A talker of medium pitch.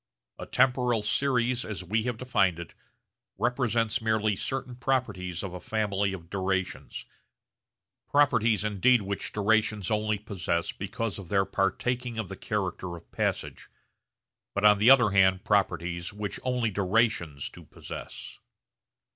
No: low, 105 Hz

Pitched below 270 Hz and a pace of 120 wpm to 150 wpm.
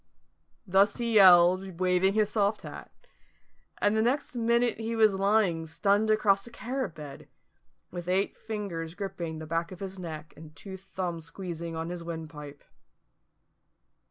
Yes: high, 190 Hz; average, 145 wpm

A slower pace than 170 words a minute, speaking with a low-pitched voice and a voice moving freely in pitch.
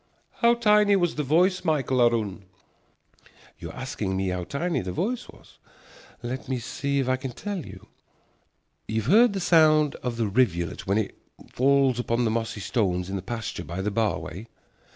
No: average, 185 wpm; low, 125 Hz; wide, 7.1 semitones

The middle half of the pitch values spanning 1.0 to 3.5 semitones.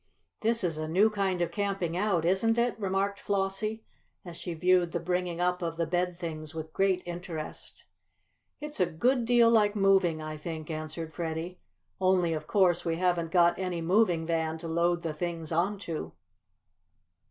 Yes: average, 2.9 semitones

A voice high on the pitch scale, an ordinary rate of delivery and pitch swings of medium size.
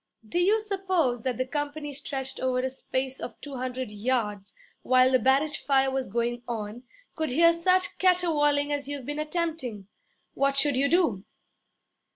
Yes: very high, 270 Hz; average, 165 wpm; average, 3.5 semitones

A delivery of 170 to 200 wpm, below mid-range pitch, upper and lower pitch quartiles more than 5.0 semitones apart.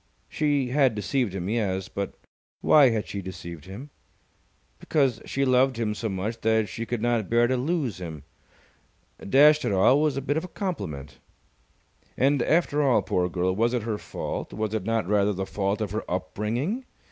Yes: average, 185 wpm; low, 115 Hz; wide, 5.5 semitones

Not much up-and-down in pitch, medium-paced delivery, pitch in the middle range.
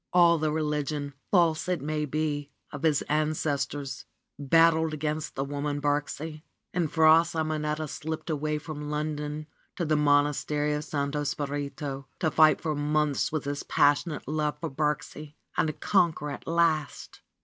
Yes: narrow, 1.3 semitones; average, 145 wpm; medium, 150 Hz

